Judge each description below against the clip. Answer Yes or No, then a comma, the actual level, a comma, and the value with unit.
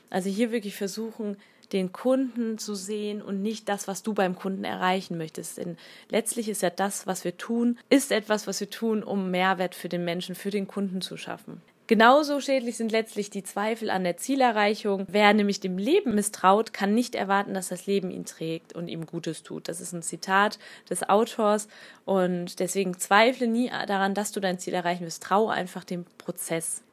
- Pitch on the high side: Yes, high, 200 Hz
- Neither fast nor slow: No, fast, 195 wpm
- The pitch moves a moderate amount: Yes, average, 3.0 semitones